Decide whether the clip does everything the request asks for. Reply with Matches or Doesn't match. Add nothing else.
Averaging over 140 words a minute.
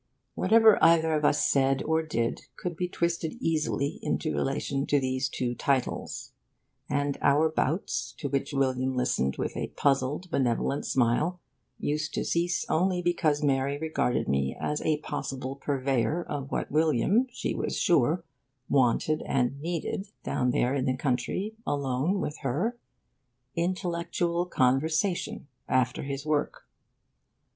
Doesn't match